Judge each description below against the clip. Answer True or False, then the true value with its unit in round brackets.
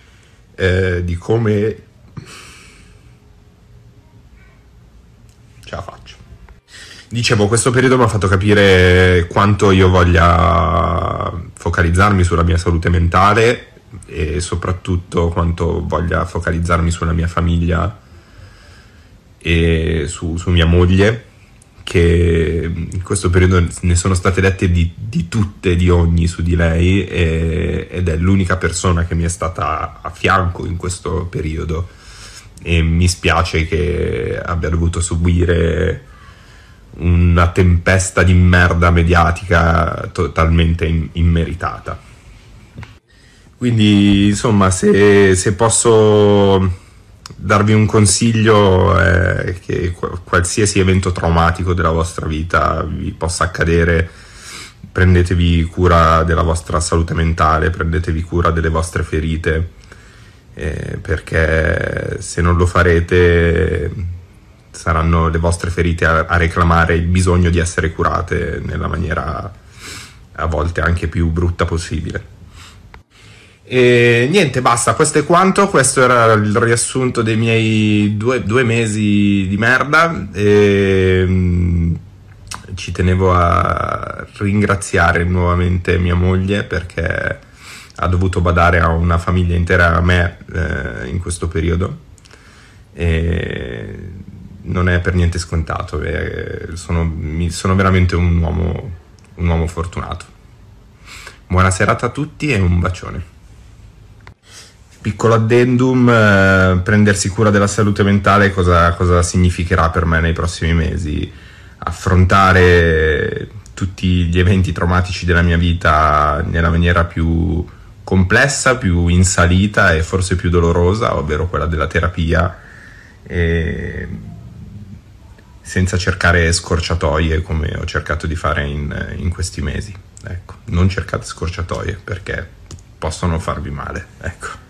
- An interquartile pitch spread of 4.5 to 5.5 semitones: False (2.9 semitones)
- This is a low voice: True (90 Hz)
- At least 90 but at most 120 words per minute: True (115 wpm)